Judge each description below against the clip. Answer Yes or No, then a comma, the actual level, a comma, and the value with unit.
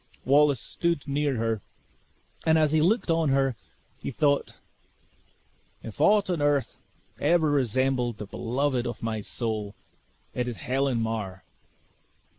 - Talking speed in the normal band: No, slow, 130 wpm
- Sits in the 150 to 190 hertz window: No, low, 135 Hz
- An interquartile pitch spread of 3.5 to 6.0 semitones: Yes, average, 4.6 semitones